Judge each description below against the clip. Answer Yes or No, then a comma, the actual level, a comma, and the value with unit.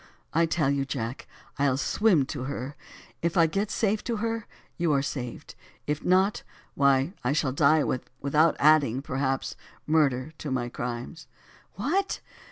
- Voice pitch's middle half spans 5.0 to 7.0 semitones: No, average, 4.2 semitones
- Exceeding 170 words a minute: No, average, 150 wpm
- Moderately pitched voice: Yes, medium, 145 Hz